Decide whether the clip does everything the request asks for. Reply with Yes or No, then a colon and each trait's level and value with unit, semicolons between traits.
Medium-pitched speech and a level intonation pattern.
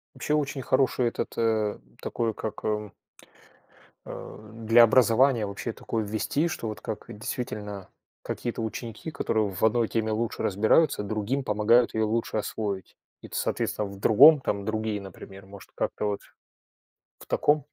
No: low, 110 Hz; narrow, 2.3 semitones